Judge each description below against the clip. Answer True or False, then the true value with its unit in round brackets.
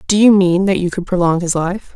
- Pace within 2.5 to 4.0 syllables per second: False (5.6 syllables/s)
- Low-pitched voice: False (185 Hz)